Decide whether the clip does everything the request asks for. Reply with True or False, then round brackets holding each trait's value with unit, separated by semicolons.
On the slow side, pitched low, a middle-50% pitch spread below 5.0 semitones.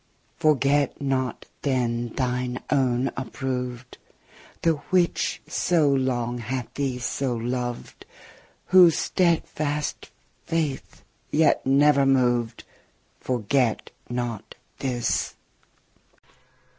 True (80 wpm; 130 Hz; 2.8 semitones)